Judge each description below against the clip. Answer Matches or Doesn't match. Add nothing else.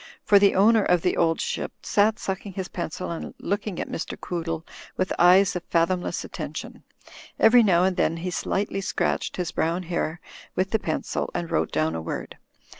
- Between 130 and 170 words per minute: Doesn't match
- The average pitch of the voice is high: Doesn't match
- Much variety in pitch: Doesn't match